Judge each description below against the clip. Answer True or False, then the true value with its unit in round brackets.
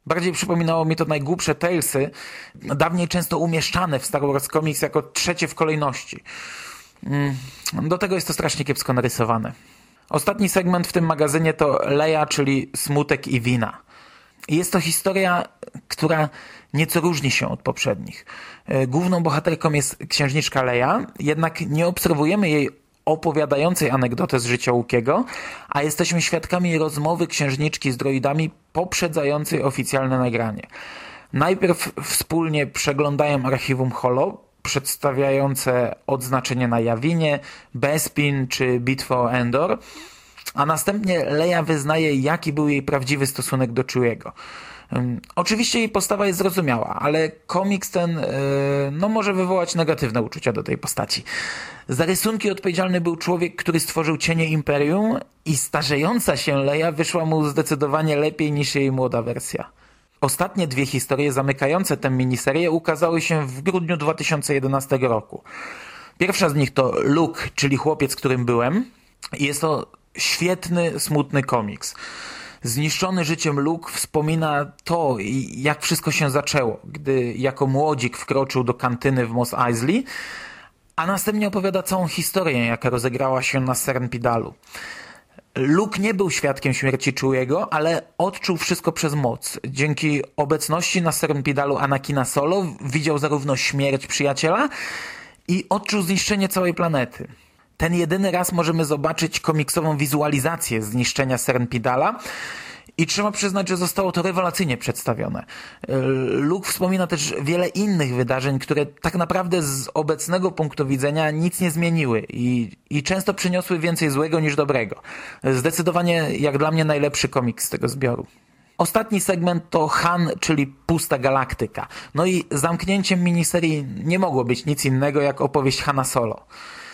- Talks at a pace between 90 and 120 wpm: False (135 wpm)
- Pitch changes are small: False (4.0 semitones)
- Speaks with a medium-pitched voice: True (155 Hz)